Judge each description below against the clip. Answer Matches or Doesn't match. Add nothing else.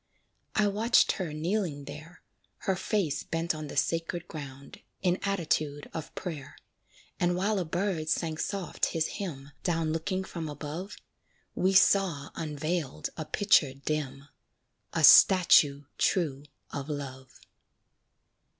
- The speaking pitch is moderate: Matches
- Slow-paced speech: Matches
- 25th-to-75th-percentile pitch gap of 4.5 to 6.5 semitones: Doesn't match